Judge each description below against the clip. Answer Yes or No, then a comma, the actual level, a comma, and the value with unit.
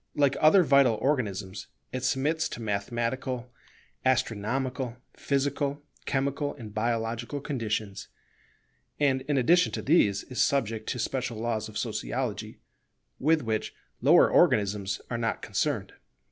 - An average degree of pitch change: Yes, average, 4.1 semitones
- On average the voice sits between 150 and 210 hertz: No, low, 125 Hz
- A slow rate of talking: Yes, slow, 120 wpm